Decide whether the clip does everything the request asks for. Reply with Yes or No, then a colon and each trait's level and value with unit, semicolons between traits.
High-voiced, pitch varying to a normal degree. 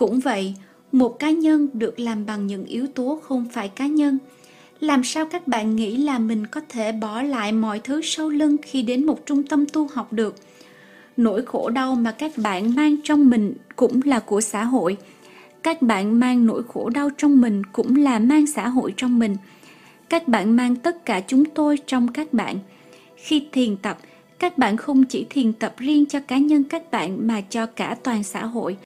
Yes: very high, 250 Hz; average, 4.5 semitones